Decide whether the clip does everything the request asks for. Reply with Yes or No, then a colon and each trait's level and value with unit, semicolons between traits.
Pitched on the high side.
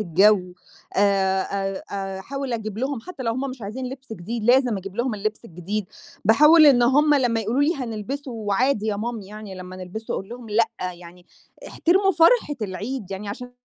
Yes: high, 220 Hz